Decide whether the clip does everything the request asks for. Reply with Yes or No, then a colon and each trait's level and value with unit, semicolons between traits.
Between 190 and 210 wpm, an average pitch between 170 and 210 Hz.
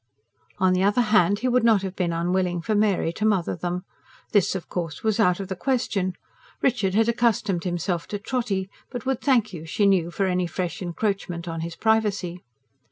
Yes: average, 195 wpm; high, 190 Hz